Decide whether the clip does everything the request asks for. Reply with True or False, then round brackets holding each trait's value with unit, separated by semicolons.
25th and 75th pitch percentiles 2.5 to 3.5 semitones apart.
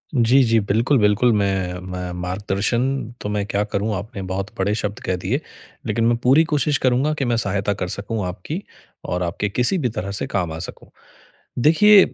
False (4.1 semitones)